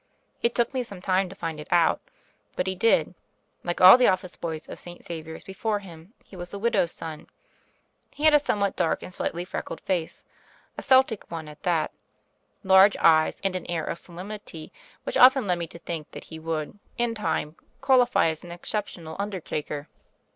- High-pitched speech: No, medium, 180 Hz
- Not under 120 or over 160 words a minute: No, average, 195 wpm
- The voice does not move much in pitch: No, average, 4.2 semitones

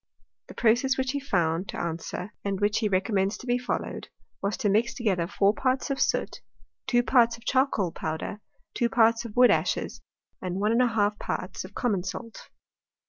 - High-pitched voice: Yes, high, 215 Hz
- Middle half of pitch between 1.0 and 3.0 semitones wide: No, average, 4.0 semitones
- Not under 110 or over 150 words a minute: No, average, 175 wpm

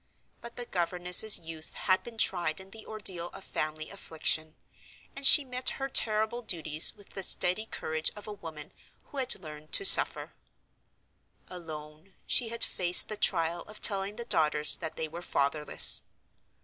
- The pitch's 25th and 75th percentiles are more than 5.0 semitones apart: Yes, wide, 5.5 semitones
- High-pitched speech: No, medium, 180 Hz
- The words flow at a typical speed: Yes, average, 160 wpm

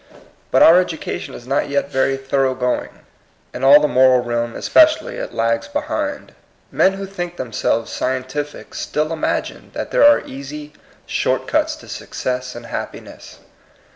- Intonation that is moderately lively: Yes, average, 4.4 semitones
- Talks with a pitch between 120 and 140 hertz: Yes, low, 135 Hz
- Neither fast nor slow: Yes, average, 155 wpm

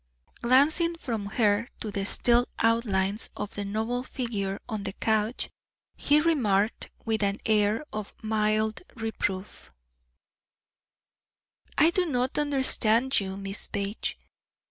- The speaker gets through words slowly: Yes, slow, 120 wpm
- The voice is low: No, high, 220 Hz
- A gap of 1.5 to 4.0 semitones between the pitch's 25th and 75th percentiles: Yes, average, 3.4 semitones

